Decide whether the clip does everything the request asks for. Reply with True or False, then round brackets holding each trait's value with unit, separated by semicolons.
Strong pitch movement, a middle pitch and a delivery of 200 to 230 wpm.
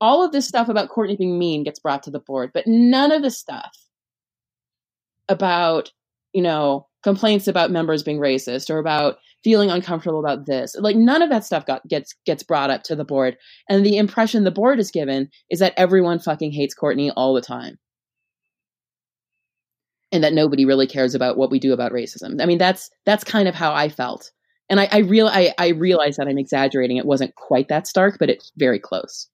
True (6.5 semitones; 160 Hz; 205 wpm)